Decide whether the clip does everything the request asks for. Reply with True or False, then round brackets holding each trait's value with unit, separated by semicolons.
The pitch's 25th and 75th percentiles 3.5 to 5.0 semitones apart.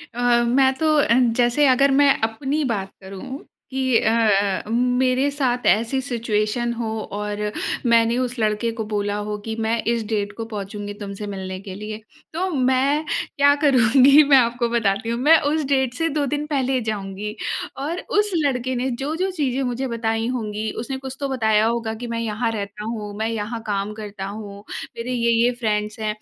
True (3.8 semitones)